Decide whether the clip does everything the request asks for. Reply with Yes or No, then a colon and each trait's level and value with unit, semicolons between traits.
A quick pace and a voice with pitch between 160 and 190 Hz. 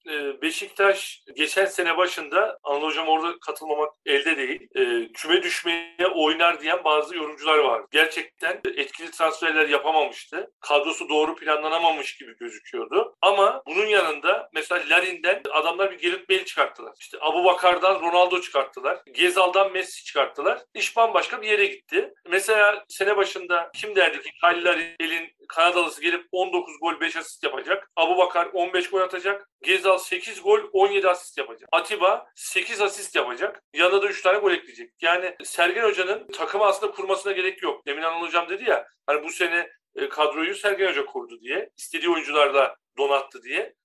Yes: fast, 150 wpm; medium, 185 Hz